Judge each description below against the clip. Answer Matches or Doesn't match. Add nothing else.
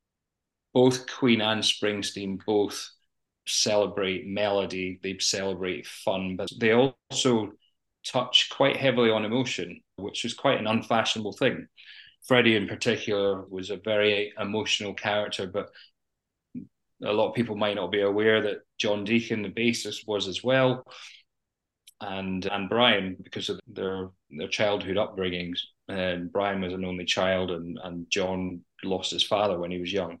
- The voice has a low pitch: Matches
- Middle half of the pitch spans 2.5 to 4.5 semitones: Matches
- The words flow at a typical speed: Matches